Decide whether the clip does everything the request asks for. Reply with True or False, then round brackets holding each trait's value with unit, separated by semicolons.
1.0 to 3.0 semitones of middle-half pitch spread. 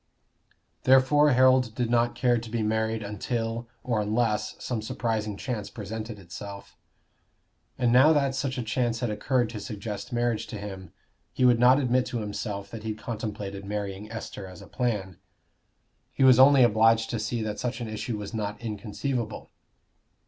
True (2.6 semitones)